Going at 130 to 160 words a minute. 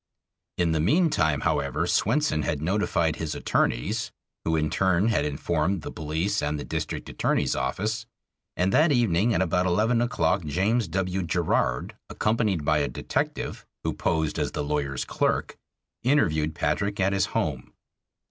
Yes: average, 150 wpm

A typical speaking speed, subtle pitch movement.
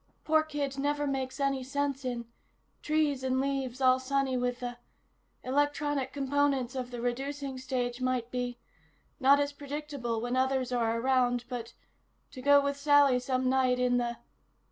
Yes: average, 155 wpm; narrow, 2.2 semitones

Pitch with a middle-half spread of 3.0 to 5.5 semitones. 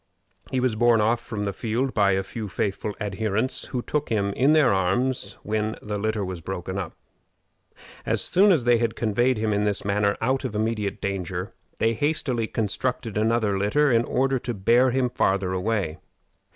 Yes: average, 3.5 semitones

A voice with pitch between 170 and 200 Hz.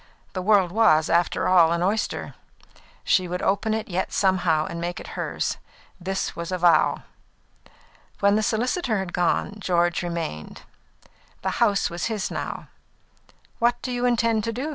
Yes: high, 190 Hz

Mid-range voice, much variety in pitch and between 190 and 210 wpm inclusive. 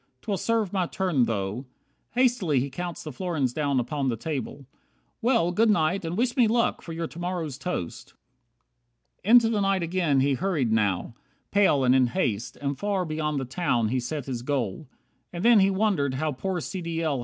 Yes: medium, 160 Hz; wide, 6.3 semitones; average, 200 wpm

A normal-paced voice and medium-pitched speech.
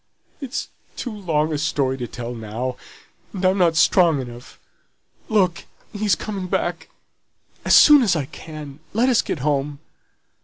Yes: average, 150 wpm; medium, 160 Hz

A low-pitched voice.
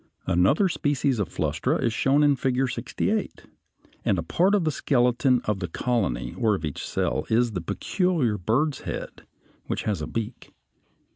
Yes: low, 125 Hz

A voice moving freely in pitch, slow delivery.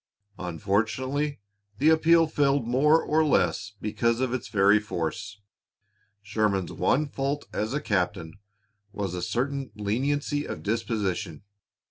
Yes: wide, 6.1 semitones; slow, 120 wpm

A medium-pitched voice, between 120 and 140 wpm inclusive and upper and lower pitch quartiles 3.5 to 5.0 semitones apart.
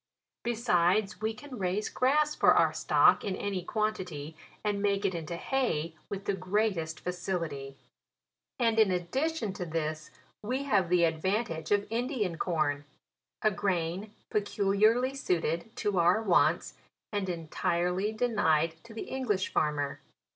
No: high, 195 Hz; slow, 135 wpm; average, 4.4 semitones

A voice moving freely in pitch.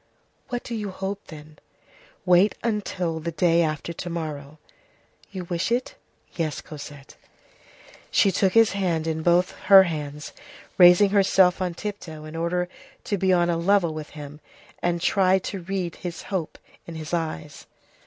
No: average, 3.3 semitones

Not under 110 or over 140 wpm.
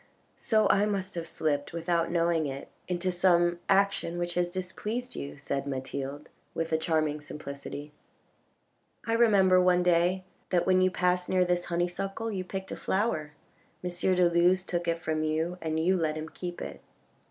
No: average, 175 wpm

